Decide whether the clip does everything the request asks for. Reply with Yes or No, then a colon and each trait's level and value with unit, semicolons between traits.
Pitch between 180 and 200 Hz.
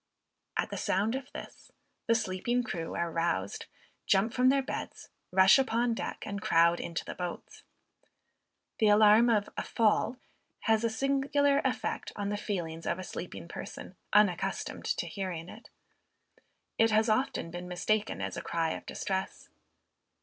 No: high, 210 Hz